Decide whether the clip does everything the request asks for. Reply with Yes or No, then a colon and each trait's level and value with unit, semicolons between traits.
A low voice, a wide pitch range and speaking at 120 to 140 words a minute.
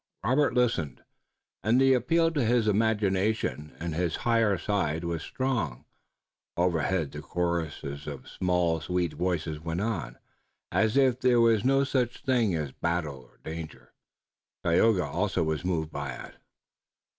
Yes: very low, 90 Hz; wide, 6.4 semitones; slow, 135 wpm